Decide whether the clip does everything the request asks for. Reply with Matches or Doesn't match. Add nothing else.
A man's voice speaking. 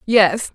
Doesn't match